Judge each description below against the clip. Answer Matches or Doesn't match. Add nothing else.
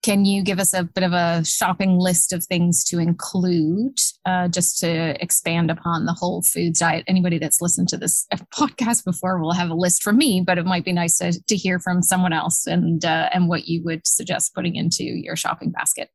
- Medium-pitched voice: Matches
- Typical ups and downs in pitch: Doesn't match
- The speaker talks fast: Matches